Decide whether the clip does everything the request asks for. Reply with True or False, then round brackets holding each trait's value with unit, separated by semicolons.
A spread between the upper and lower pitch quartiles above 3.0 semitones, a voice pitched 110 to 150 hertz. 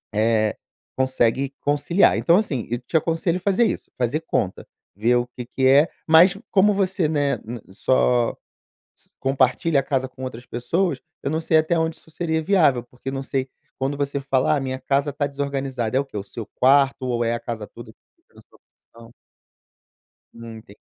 True (4.5 semitones; 135 Hz)